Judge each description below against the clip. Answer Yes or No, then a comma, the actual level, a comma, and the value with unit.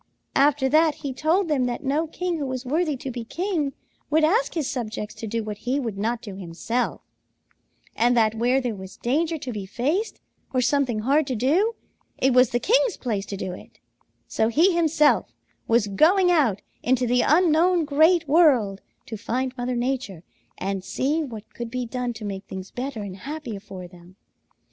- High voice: Yes, very high, 255 Hz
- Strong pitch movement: Yes, wide, 5.7 semitones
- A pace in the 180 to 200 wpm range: Yes, average, 185 wpm